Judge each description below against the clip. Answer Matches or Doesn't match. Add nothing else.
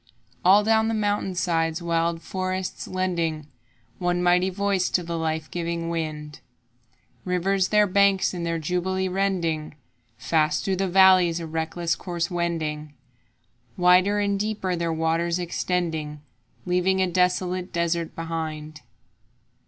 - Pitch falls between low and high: Matches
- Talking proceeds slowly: Matches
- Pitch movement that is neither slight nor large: Doesn't match